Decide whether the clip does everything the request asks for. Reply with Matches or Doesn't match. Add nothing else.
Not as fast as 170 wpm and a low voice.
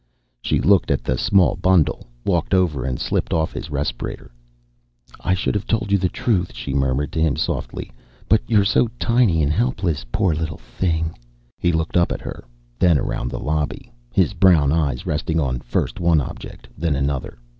Doesn't match